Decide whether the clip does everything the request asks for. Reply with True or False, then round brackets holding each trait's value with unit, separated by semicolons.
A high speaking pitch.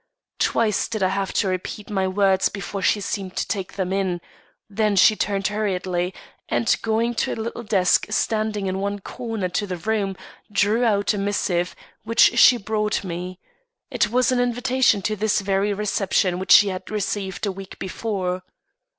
True (200 Hz)